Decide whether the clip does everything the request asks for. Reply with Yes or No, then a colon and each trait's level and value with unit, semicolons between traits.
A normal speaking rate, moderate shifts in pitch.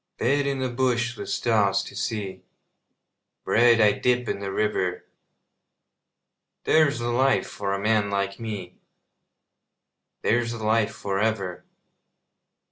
No: slow, 125 wpm; average, 3.4 semitones